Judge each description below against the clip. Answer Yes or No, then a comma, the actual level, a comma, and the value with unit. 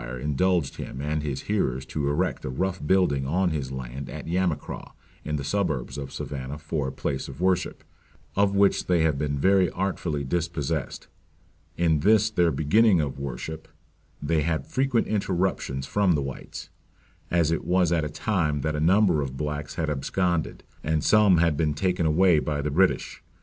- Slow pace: No, average, 175 wpm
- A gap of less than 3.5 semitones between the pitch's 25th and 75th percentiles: No, average, 4.2 semitones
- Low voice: Yes, very low, 80 Hz